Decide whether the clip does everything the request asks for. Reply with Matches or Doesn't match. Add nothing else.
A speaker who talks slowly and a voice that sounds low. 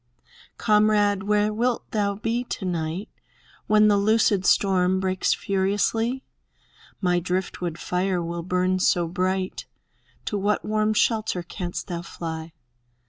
Doesn't match